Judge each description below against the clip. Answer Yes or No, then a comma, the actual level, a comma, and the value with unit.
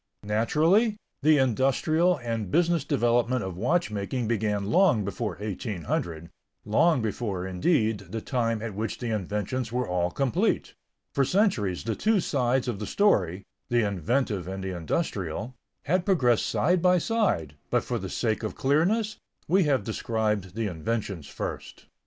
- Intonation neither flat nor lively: No, wide, 6.4 semitones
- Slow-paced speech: No, average, 145 wpm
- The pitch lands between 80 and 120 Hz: Yes, low, 115 Hz